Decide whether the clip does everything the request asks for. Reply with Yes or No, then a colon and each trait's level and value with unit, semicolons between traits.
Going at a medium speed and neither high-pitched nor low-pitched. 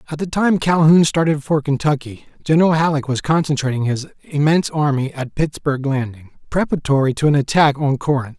Yes: average, 165 wpm; medium, 145 Hz